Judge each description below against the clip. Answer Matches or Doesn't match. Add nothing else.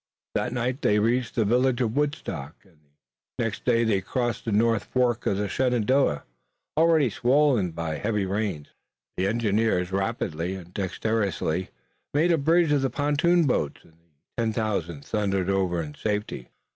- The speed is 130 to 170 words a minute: Matches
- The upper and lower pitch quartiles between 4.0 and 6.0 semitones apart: Matches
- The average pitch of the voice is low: Matches